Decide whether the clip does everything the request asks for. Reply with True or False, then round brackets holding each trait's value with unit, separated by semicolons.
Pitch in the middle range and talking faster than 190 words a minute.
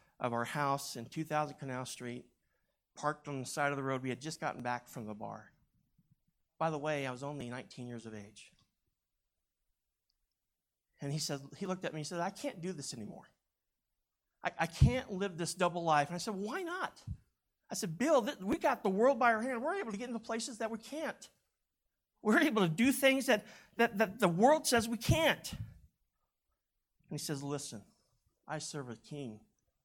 True (155 Hz; 200 wpm)